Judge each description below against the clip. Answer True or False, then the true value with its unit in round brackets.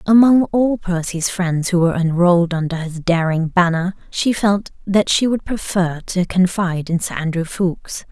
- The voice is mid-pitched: True (180 Hz)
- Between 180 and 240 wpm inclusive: False (170 wpm)